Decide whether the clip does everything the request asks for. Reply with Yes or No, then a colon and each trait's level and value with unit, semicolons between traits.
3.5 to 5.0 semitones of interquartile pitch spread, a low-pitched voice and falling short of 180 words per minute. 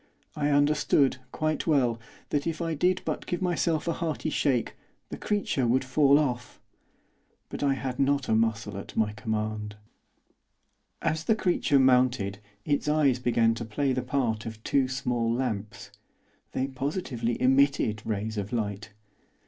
Yes: average, 4.4 semitones; low, 130 Hz; average, 150 wpm